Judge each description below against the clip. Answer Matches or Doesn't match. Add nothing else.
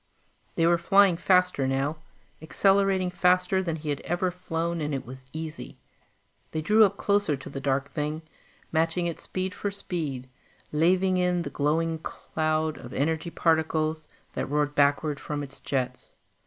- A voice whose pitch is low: Doesn't match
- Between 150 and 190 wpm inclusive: Matches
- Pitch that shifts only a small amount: Doesn't match